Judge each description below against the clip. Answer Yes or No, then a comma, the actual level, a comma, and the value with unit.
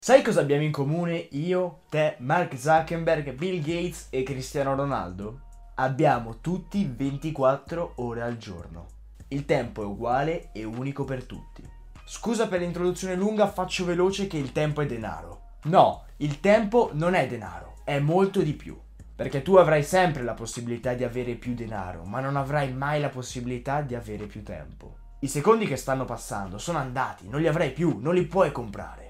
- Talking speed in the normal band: No, fast, 175 wpm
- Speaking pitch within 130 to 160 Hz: Yes, medium, 140 Hz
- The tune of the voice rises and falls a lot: Yes, wide, 6.4 semitones